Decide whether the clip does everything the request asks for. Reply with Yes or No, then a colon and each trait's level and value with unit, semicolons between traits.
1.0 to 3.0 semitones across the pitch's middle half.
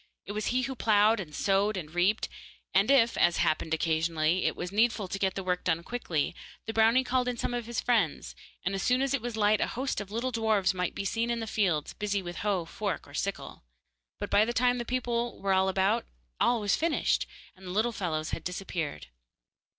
No: average, 4.6 semitones